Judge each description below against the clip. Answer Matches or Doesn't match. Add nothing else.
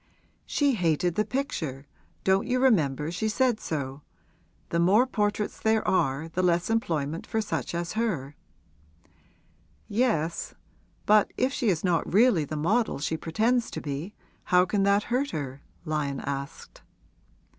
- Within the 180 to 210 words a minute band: Doesn't match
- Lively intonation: Matches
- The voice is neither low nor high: Matches